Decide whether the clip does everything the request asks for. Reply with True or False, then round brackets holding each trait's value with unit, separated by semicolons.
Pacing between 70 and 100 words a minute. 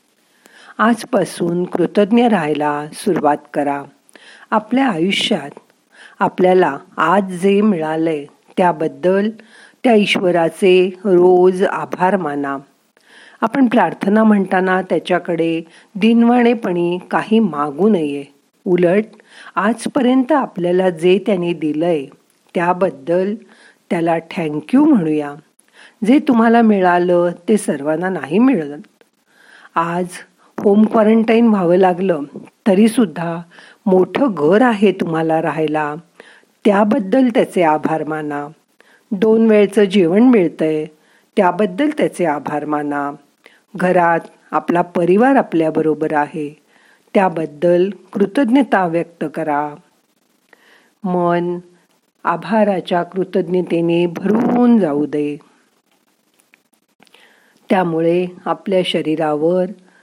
True (85 wpm)